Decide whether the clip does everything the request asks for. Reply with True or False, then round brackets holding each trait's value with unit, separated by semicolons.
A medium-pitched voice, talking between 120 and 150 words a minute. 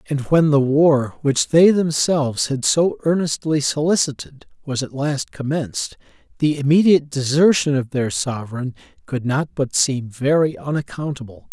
True (145 Hz; 140 wpm)